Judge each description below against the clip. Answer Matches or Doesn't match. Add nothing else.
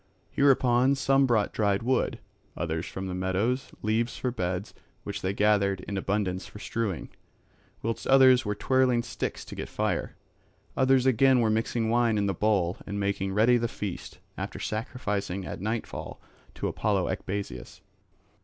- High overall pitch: Doesn't match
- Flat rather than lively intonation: Doesn't match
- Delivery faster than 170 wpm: Doesn't match